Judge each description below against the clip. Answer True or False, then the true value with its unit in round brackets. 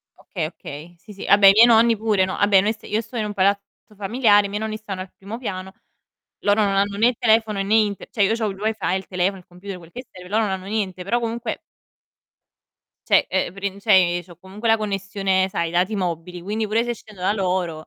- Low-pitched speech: False (200 Hz)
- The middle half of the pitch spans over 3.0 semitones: False (2.6 semitones)